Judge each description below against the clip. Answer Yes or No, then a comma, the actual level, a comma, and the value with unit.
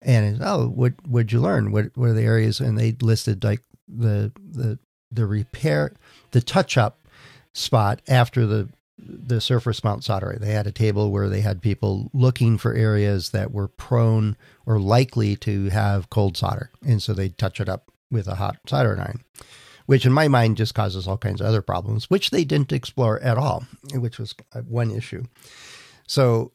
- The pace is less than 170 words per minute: No, average, 185 wpm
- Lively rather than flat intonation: No, average, 2.9 semitones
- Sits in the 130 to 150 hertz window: No, low, 115 Hz